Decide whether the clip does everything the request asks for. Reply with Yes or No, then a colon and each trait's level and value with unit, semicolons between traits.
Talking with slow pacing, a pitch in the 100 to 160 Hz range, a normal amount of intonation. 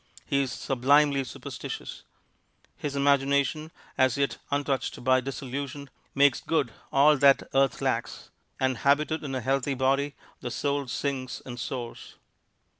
No: slow, 130 wpm; low, 135 Hz; narrow, 1.4 semitones